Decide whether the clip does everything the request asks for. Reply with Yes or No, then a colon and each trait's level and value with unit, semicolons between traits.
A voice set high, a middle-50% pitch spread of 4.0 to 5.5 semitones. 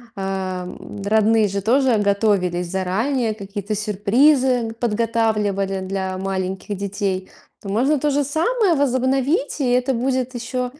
Yes: high, 220 Hz; average, 4.8 semitones